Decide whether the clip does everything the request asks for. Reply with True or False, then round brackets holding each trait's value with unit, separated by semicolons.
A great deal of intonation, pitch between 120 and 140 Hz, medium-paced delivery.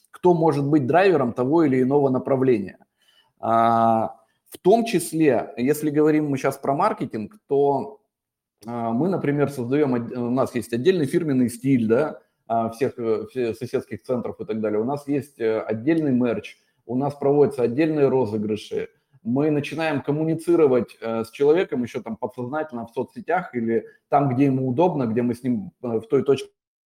False (4.4 semitones; 135 Hz; 145 wpm)